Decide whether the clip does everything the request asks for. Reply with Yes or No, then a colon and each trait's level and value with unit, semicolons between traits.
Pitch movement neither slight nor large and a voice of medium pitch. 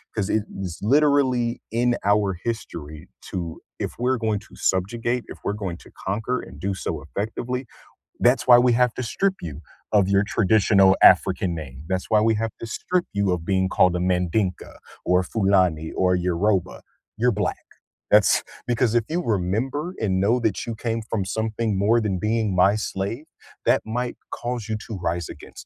No: average, 4.0 semitones; low, 105 Hz